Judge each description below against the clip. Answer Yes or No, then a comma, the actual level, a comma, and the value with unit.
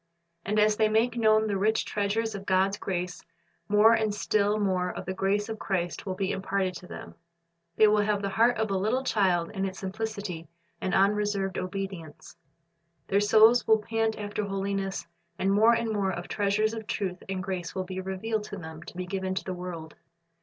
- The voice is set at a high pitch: Yes, high, 200 Hz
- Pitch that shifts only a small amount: Yes, narrow, 2.3 semitones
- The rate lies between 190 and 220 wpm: Yes, average, 200 wpm